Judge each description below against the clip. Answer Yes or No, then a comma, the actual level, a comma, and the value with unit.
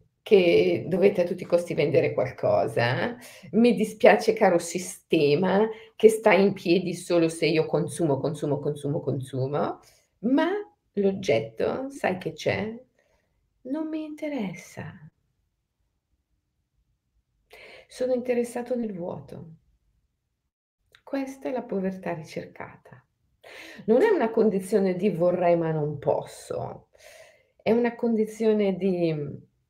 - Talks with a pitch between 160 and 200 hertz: Yes, high, 190 Hz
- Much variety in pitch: Yes, wide, 6.3 semitones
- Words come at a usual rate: No, slow, 105 wpm